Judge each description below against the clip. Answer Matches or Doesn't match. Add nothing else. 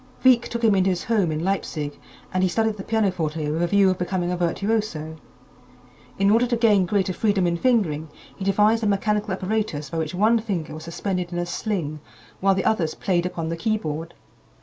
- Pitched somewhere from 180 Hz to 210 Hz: Matches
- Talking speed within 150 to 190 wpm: Doesn't match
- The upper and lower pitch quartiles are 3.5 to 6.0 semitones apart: Matches